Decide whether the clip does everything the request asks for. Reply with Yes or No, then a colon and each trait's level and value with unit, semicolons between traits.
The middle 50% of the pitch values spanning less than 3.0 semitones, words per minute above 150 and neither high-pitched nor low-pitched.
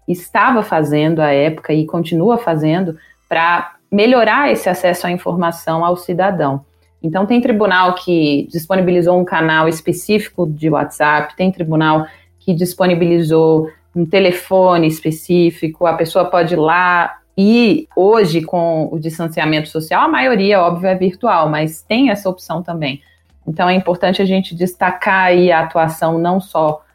No: narrow, 2.6 semitones; average, 145 wpm; medium, 175 Hz